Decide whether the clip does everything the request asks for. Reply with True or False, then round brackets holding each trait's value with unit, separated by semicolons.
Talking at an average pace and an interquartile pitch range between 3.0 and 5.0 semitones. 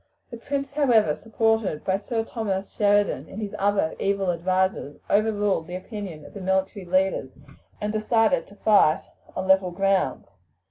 False (150 wpm; 2.6 semitones)